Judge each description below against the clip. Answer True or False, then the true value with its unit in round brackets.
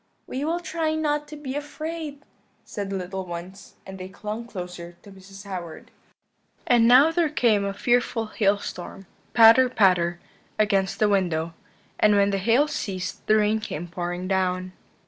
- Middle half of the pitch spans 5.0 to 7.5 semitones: True (5.3 semitones)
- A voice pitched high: True (205 Hz)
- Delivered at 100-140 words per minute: False (160 wpm)